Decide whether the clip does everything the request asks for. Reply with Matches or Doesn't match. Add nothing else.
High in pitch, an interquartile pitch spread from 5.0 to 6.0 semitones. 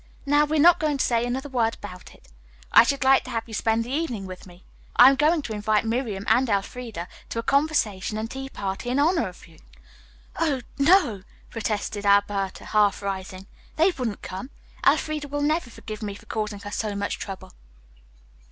Matches